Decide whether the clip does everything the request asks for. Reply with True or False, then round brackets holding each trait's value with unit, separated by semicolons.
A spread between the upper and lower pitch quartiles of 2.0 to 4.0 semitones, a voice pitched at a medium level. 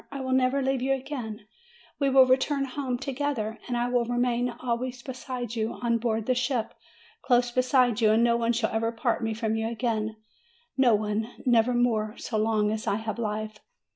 False (2.4 semitones; 240 Hz)